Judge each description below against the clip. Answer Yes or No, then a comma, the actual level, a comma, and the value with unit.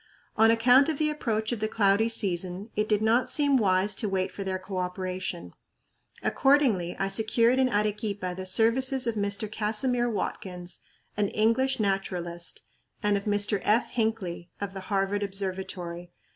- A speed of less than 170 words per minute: Yes, average, 155 wpm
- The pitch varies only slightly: No, average, 3.3 semitones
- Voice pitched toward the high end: Yes, high, 205 Hz